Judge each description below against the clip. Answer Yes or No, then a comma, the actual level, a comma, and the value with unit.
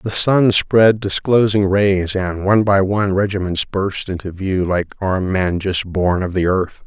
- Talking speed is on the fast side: No, average, 185 wpm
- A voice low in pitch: Yes, very low, 95 Hz